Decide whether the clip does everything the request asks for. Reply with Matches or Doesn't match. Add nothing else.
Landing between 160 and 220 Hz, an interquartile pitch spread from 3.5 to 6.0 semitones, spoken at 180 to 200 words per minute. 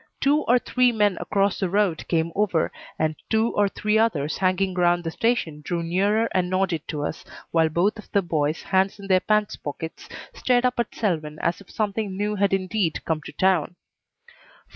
Matches